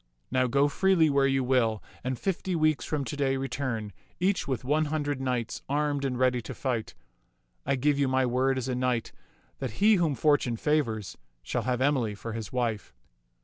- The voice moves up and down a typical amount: Yes, average, 3.0 semitones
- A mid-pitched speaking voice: No, low, 130 Hz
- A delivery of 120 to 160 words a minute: No, average, 190 wpm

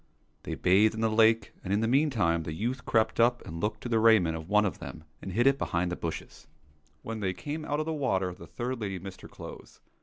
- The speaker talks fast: Yes, fast, 240 wpm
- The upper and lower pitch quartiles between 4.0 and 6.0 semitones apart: Yes, average, 4.7 semitones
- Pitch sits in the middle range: No, low, 110 Hz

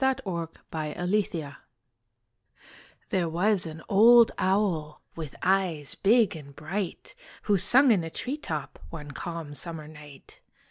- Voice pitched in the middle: Yes, medium, 170 Hz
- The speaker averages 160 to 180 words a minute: No, average, 140 wpm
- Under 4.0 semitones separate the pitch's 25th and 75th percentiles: No, average, 4.7 semitones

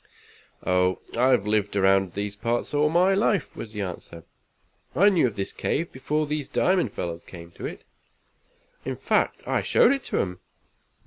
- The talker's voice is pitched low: Yes, low, 110 Hz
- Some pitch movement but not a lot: No, wide, 7.9 semitones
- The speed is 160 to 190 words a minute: Yes, average, 170 wpm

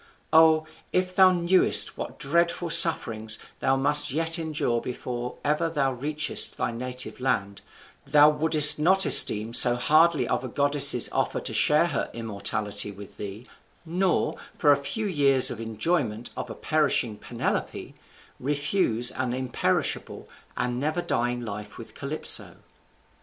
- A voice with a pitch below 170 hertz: Yes, medium, 140 Hz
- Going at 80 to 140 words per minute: Yes, slow, 135 wpm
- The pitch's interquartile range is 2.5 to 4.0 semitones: No, average, 5.0 semitones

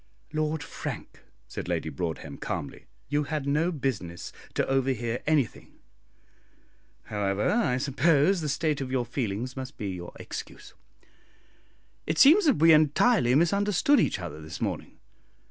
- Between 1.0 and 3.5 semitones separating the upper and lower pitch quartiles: No, wide, 5.4 semitones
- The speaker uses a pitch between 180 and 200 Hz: No, medium, 140 Hz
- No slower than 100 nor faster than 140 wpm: Yes, slow, 135 wpm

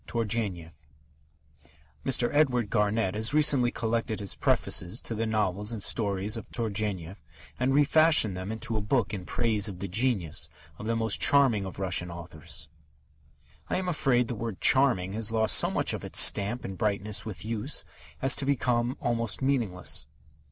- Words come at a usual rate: Yes, average, 170 wpm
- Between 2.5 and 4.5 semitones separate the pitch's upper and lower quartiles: Yes, average, 3.6 semitones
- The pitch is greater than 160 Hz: No, low, 110 Hz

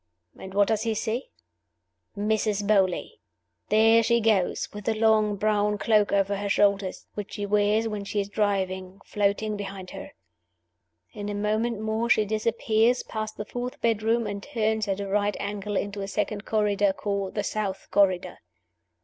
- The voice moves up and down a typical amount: No, narrow, 1.4 semitones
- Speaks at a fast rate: No, average, 165 wpm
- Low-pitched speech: No, high, 210 Hz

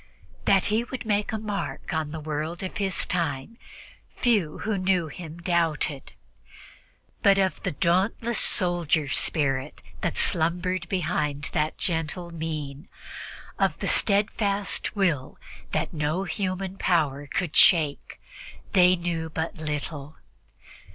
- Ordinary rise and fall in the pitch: Yes, average, 3.9 semitones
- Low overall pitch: No, medium, 170 Hz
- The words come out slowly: Yes, slow, 125 wpm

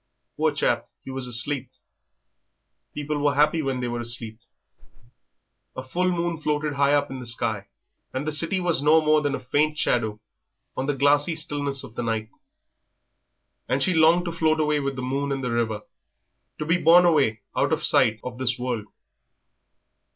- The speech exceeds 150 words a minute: Yes, average, 180 wpm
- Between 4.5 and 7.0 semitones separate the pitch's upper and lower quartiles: No, average, 3.7 semitones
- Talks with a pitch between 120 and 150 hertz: Yes, medium, 140 Hz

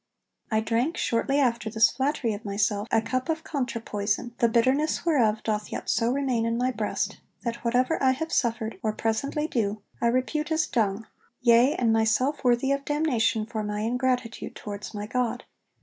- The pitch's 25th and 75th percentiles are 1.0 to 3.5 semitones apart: Yes, average, 3.0 semitones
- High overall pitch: Yes, high, 235 Hz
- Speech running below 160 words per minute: No, average, 180 wpm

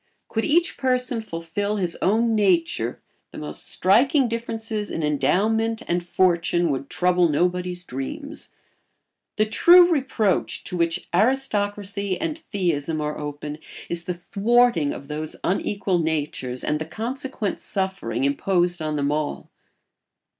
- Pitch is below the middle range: No, medium, 185 Hz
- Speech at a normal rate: No, slow, 130 wpm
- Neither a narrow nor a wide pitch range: No, wide, 6.0 semitones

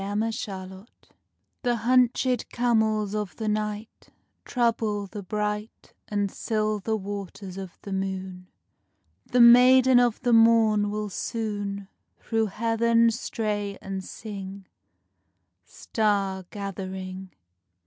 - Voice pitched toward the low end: No, high, 210 Hz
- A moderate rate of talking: No, slow, 105 wpm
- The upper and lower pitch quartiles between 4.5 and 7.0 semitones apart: No, narrow, 2.6 semitones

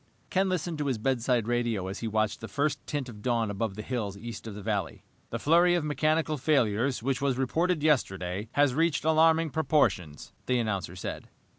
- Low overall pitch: Yes, low, 125 Hz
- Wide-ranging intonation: Yes, wide, 6.1 semitones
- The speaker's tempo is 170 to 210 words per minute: Yes, average, 190 wpm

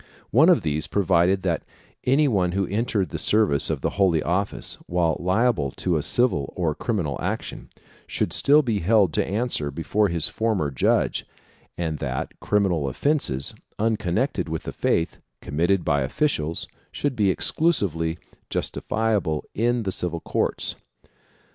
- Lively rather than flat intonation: Yes, wide, 5.7 semitones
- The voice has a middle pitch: No, very low, 95 Hz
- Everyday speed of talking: Yes, average, 145 wpm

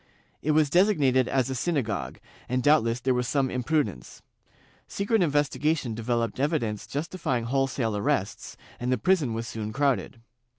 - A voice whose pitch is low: Yes, low, 130 Hz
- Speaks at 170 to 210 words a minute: No, average, 155 wpm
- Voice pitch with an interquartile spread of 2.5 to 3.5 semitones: No, average, 4.4 semitones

